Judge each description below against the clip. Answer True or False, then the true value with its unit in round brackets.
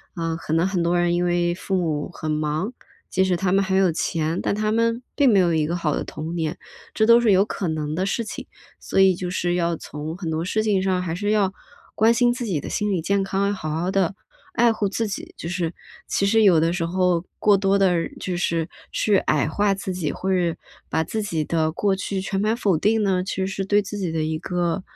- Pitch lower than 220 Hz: True (185 Hz)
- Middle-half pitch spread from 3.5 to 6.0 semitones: False (3.1 semitones)